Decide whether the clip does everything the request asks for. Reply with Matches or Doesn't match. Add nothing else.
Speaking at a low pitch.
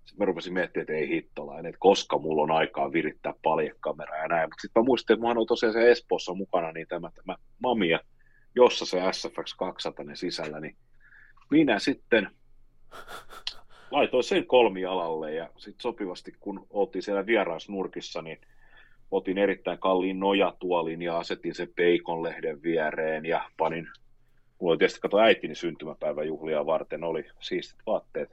Matches